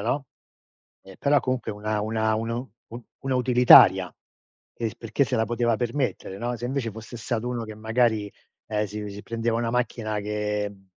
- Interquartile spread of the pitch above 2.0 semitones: Yes, narrow, 2.4 semitones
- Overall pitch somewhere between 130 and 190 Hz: No, low, 115 Hz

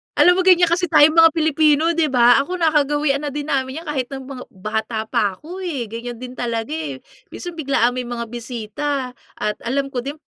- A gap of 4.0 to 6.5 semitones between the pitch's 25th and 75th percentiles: Yes, average, 4.6 semitones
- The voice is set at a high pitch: Yes, very high, 275 Hz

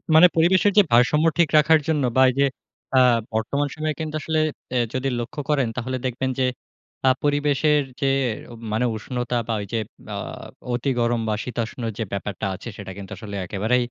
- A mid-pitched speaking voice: No, low, 130 Hz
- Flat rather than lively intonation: No, average, 4.4 semitones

